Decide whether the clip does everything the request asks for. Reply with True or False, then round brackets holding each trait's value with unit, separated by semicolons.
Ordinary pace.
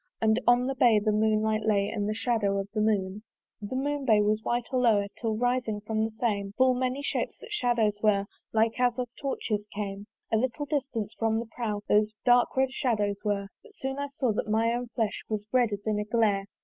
False (225 wpm)